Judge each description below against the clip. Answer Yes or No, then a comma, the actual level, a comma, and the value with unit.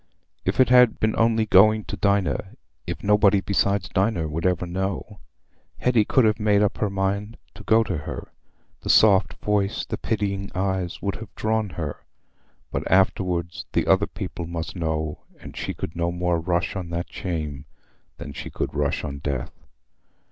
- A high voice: No, very low, 95 Hz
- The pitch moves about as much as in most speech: Yes, average, 3.5 semitones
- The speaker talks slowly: No, average, 165 wpm